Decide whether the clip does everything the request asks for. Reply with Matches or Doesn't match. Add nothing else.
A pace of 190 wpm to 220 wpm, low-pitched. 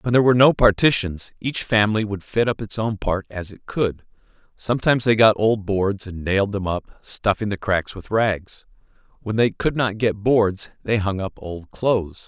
Matches